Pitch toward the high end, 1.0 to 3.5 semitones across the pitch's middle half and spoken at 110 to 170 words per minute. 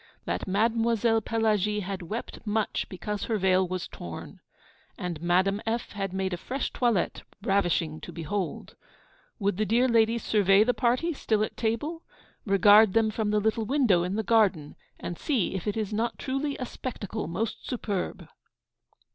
Yes: high, 210 Hz; average, 3.2 semitones; average, 165 wpm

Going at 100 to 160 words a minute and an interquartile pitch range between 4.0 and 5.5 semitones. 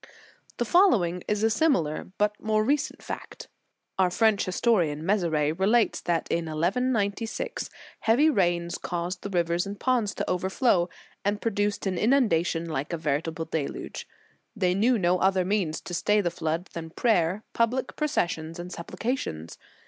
Yes: average, 155 wpm; average, 4.6 semitones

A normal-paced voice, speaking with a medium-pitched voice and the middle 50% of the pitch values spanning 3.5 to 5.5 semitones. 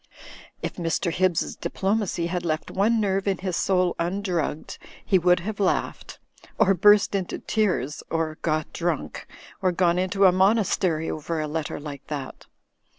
No: average, 150 wpm; medium, 180 Hz; average, 3.1 semitones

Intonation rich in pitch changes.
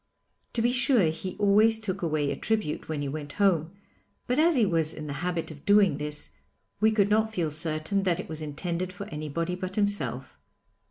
No: average, 5.0 semitones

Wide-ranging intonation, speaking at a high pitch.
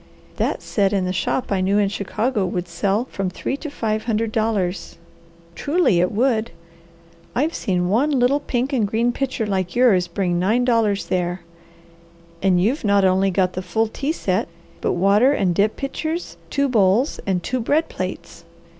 No: average, 4.9 semitones; high, 205 Hz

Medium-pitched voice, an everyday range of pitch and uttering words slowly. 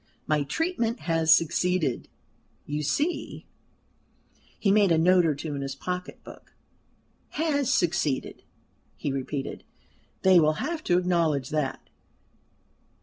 Yes: medium, 165 Hz; average, 4.3 semitones; slow, 120 wpm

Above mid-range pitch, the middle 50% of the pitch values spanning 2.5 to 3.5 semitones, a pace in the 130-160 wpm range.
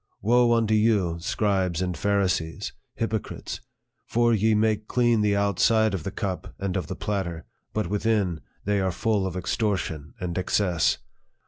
No: low, 100 Hz; average, 3.2 semitones; average, 155 wpm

